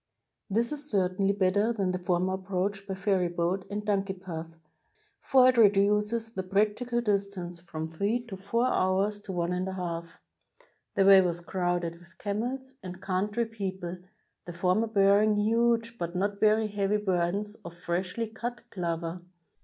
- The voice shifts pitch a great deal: No, average, 2.8 semitones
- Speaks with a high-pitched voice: Yes, high, 195 Hz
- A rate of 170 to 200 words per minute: No, average, 160 wpm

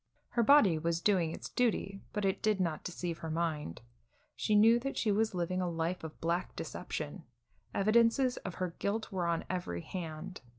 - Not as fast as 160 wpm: No, average, 180 wpm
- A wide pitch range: No, average, 4.2 semitones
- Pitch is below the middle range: No, medium, 185 Hz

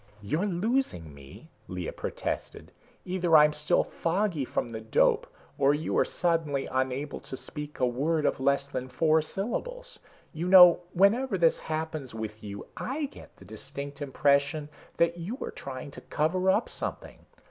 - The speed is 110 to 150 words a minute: No, average, 160 wpm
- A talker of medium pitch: Yes, medium, 150 Hz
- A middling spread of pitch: Yes, average, 5.0 semitones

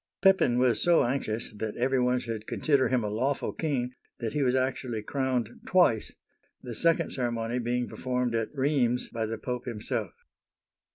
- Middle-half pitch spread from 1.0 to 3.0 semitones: Yes, narrow, 2.4 semitones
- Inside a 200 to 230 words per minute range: No, average, 165 wpm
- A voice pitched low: Yes, low, 125 Hz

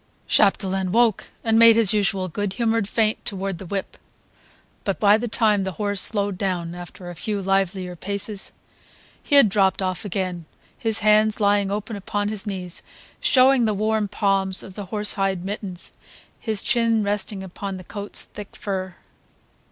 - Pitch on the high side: Yes, high, 200 Hz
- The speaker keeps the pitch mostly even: Yes, narrow, 2.0 semitones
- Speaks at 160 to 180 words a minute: Yes, average, 165 wpm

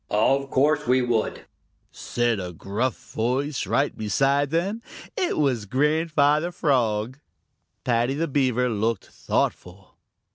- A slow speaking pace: Yes, slow, 115 wpm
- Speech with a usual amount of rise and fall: Yes, average, 4.4 semitones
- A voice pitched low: Yes, low, 130 Hz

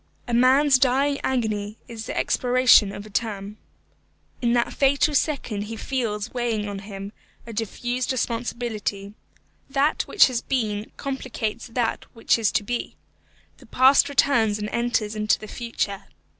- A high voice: Yes, high, 235 Hz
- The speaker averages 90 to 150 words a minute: Yes, average, 145 wpm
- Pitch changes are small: No, average, 3.4 semitones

